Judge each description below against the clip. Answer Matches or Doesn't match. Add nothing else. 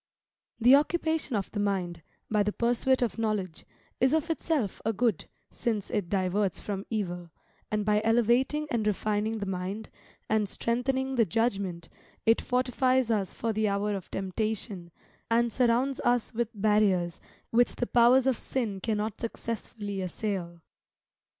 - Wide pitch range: Doesn't match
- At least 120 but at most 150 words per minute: Matches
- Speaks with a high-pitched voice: Matches